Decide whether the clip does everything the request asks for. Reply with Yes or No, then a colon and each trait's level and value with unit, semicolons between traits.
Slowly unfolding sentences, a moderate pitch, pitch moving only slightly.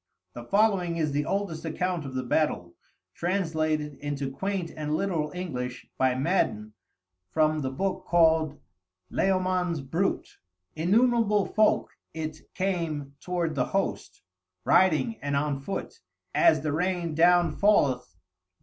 No: slow, 125 wpm; medium, 160 Hz; average, 4.1 semitones